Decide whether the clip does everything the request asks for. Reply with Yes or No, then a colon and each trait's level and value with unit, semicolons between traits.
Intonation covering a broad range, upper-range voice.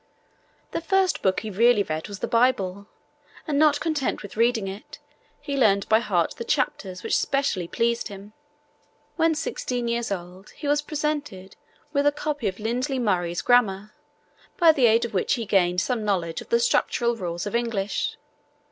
Yes: wide, 6.0 semitones; high, 230 Hz